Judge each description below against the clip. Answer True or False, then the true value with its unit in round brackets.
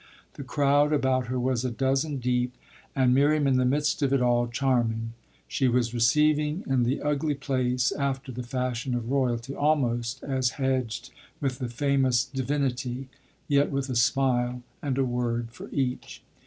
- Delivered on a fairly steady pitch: True (2.1 semitones)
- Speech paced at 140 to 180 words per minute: True (165 wpm)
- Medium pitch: False (130 Hz)